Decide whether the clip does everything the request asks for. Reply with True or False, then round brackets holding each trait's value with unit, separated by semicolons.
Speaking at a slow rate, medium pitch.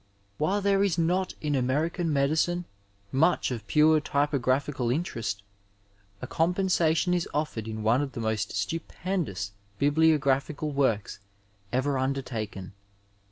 True (120 wpm; 145 Hz)